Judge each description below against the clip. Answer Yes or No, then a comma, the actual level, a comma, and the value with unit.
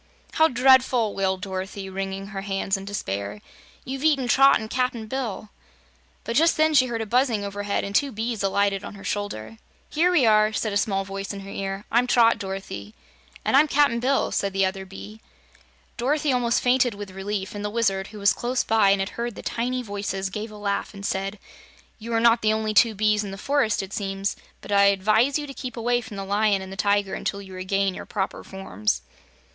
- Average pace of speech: No, fast, 215 wpm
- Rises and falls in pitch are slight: No, average, 3.5 semitones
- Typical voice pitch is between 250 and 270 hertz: No, high, 210 Hz